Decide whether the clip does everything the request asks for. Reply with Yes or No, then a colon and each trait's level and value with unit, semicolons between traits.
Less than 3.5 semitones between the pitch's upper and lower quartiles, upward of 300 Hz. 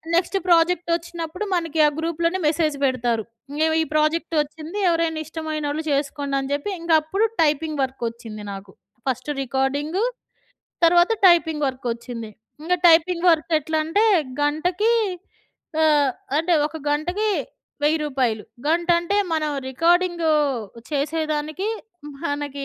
Yes: average, 2.8 semitones; very high, 310 Hz